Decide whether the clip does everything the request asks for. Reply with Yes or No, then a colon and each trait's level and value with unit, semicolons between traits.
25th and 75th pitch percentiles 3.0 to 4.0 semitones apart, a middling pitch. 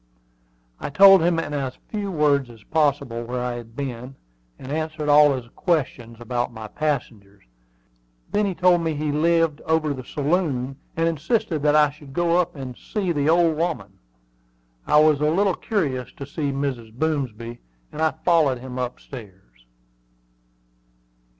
No: average, 4.5 semitones; medium, 145 Hz